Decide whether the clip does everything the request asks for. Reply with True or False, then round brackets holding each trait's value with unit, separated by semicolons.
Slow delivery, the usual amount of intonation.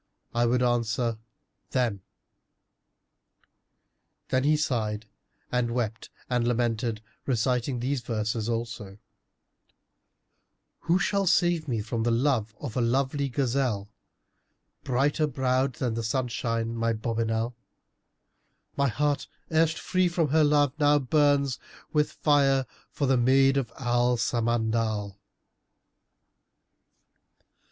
True (110 wpm; 3.4 semitones)